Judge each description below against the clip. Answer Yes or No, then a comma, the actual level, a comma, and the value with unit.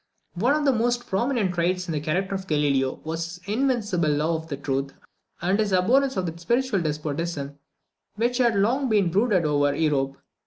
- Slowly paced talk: No, average, 180 wpm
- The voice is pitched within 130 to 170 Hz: No, medium, 180 Hz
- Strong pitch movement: Yes, wide, 7.2 semitones